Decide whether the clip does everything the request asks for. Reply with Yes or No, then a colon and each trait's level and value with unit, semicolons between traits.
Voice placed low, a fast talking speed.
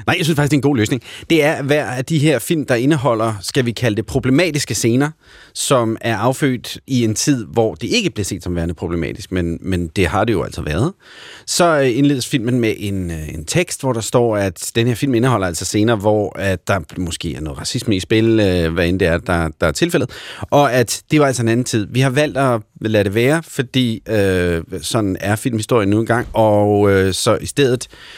Yes: low, 115 Hz; fast, 230 wpm